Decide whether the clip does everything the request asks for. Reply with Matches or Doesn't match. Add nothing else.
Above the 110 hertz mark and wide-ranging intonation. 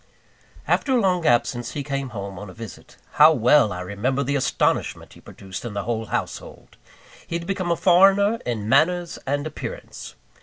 Matches